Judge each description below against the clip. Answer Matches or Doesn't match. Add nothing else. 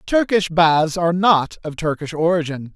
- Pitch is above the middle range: Doesn't match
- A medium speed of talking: Matches